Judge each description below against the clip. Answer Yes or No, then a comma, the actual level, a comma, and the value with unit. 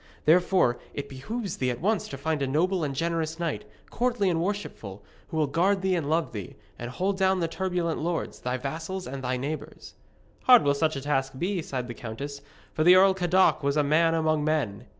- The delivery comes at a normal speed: No, fast, 210 wpm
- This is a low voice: No, medium, 160 Hz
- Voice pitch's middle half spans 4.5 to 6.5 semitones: Yes, average, 4.9 semitones